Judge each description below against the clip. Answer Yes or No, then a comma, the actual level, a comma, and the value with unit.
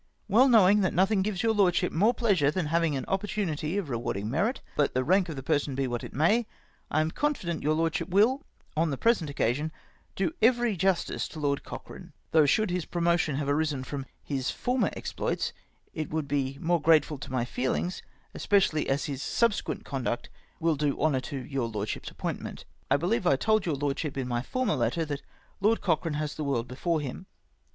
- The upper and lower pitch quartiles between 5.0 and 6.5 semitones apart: Yes, wide, 5.5 semitones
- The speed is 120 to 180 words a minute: No, average, 200 wpm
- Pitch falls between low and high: Yes, medium, 155 Hz